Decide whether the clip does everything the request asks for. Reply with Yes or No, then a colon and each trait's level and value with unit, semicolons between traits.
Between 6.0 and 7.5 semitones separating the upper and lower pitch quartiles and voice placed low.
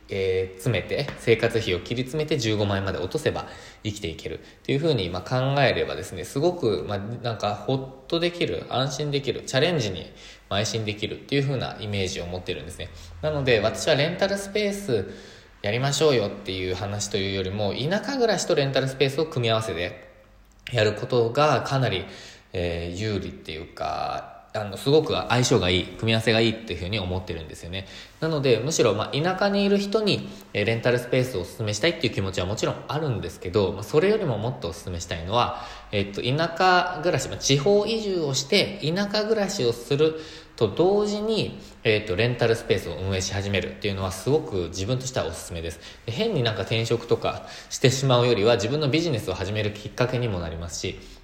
Yes: wide, 7.0 semitones; low, 115 Hz